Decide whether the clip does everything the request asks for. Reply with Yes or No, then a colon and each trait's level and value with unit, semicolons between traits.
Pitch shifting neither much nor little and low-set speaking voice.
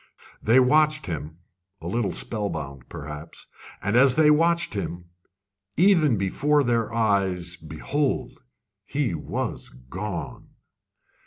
No: wide, 8.5 semitones; low, 105 Hz